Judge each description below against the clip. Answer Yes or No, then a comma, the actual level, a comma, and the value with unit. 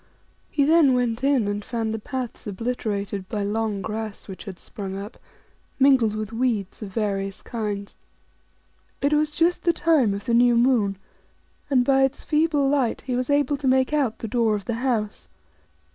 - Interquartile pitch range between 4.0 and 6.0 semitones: Yes, average, 4.4 semitones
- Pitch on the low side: No, high, 235 Hz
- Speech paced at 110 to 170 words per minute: No, average, 180 wpm